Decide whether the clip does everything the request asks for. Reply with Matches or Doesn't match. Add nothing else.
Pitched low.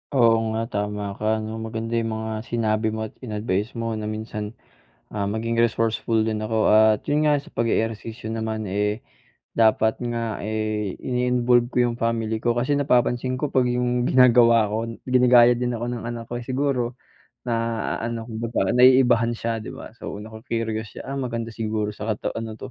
Matches